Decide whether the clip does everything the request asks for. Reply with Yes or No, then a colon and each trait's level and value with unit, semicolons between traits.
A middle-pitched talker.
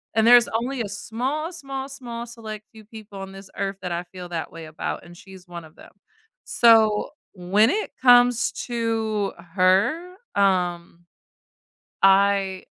No: high, 210 Hz